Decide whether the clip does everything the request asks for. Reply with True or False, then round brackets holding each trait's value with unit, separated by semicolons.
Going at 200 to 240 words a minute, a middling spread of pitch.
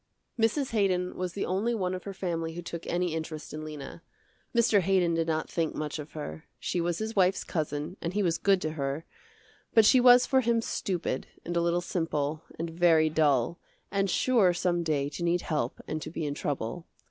True (205 wpm; 3.5 semitones)